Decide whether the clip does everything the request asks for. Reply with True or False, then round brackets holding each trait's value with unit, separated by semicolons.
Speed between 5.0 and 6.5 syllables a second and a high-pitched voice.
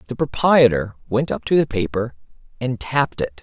False (5.3 syllables/s; 120 Hz)